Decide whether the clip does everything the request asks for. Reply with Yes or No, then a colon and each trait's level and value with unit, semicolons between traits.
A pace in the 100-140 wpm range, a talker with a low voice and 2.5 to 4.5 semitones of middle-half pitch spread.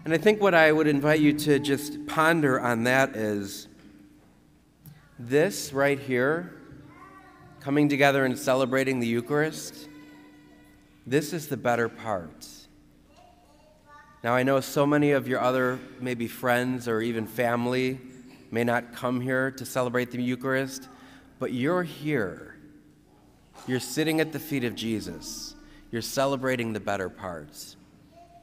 Yes: slow, 135 wpm; low, 130 Hz; average, 3.5 semitones